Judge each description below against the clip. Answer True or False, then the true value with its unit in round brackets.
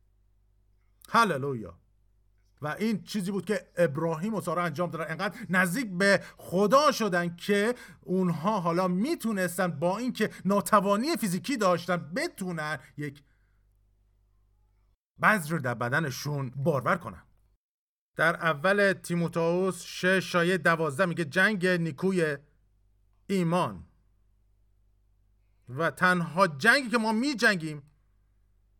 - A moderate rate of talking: False (100 wpm)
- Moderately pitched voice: True (170 Hz)